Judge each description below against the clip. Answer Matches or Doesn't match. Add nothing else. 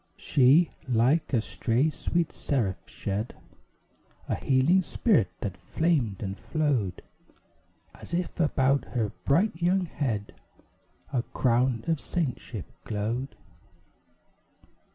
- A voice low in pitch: Matches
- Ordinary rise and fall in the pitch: Doesn't match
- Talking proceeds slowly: Matches